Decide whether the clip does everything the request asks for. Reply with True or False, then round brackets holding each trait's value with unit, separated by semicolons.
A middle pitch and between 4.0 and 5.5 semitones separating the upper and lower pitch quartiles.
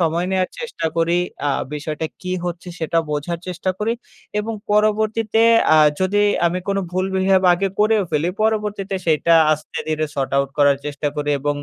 True (180 Hz; 4.8 semitones)